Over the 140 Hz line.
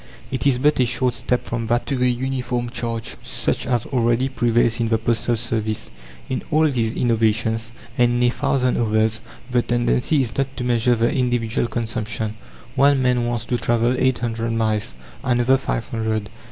No: low, 120 Hz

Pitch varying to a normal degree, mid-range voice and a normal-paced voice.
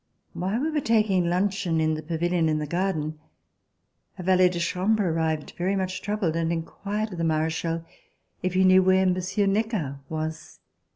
Yes: average, 3.1 semitones; medium, 180 Hz; average, 170 wpm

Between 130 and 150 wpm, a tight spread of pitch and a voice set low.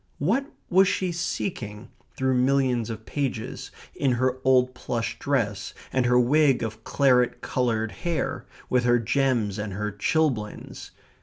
No: average, 140 wpm; average, 3.7 semitones; low, 125 Hz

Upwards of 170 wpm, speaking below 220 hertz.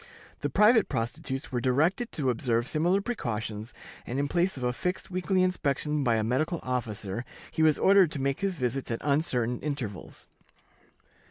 No: average, 165 wpm; medium, 140 Hz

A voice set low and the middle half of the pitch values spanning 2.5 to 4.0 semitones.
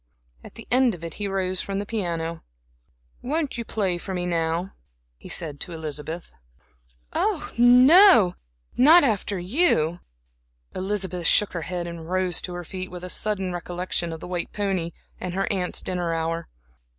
No: medium, 180 Hz; average, 3.4 semitones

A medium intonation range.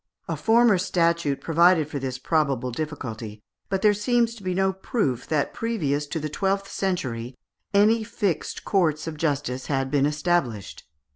No: wide, 5.9 semitones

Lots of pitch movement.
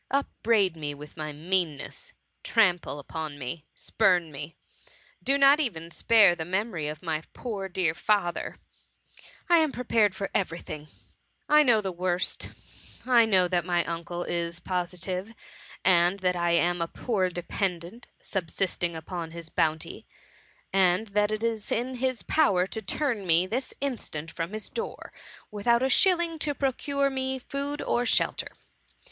Yes: wide, 5.7 semitones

